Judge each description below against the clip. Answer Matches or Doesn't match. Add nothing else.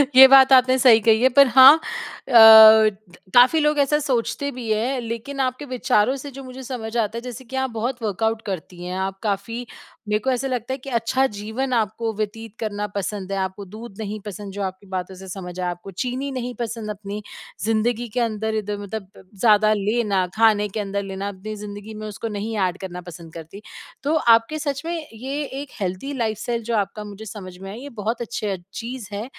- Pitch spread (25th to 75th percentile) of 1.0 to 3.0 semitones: Doesn't match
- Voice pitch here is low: Doesn't match